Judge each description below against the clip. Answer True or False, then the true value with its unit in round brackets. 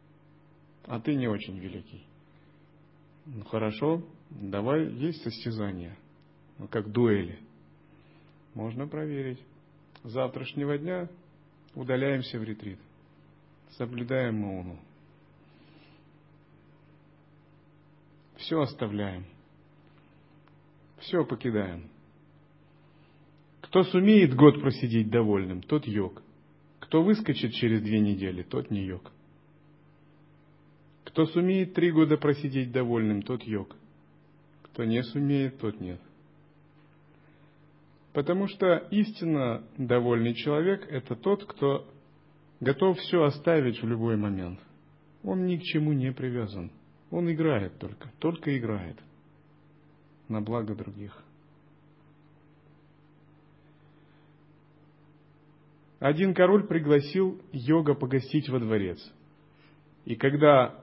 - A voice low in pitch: False (145 Hz)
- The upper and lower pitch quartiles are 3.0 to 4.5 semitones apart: False (5.1 semitones)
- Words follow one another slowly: True (90 wpm)